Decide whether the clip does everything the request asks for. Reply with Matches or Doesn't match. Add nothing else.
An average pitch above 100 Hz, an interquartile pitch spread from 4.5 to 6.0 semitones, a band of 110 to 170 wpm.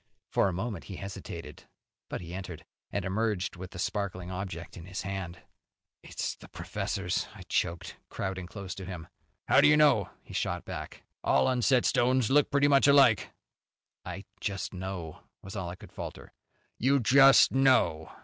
Doesn't match